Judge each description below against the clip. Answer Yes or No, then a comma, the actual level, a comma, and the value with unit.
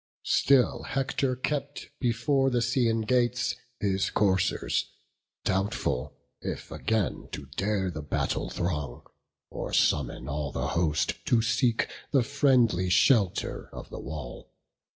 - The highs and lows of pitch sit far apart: Yes, wide, 6.6 semitones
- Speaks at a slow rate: Yes, slow, 120 wpm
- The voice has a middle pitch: No, low, 110 Hz